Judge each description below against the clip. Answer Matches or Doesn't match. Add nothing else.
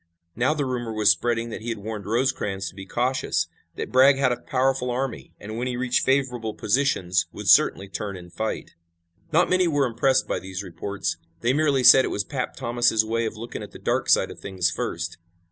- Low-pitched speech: Matches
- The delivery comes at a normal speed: Doesn't match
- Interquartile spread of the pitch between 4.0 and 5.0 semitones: Matches